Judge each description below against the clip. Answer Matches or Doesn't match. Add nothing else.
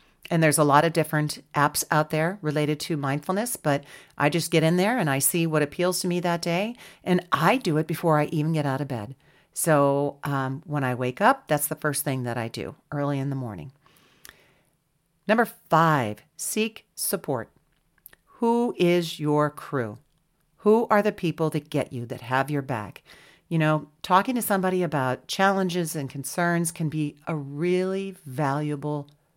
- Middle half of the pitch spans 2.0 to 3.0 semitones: Doesn't match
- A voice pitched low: Doesn't match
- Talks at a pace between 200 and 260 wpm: Doesn't match